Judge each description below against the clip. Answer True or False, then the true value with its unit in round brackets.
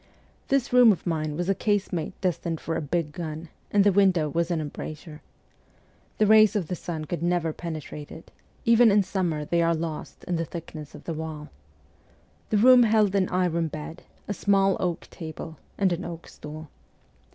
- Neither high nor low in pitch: True (170 Hz)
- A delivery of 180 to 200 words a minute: True (185 wpm)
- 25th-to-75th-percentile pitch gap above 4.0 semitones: False (3.7 semitones)